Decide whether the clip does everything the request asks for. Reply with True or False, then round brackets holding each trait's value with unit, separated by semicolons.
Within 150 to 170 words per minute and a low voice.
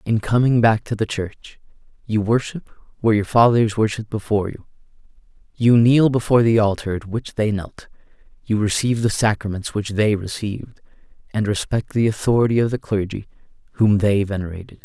True (160 wpm; 110 Hz)